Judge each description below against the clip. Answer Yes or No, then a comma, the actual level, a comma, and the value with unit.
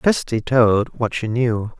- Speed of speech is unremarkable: Yes, average, 165 wpm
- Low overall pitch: Yes, low, 115 Hz